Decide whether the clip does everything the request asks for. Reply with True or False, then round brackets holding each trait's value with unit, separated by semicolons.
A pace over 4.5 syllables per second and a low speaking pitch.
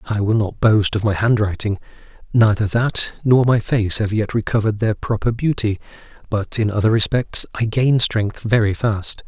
True (4.9 syllables/s; 110 Hz)